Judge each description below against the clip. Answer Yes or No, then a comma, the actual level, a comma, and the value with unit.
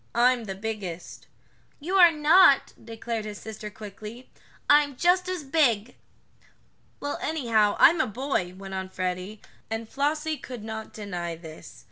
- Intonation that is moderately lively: No, wide, 6.1 semitones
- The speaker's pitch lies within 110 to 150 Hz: No, high, 225 Hz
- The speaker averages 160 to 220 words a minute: No, average, 140 wpm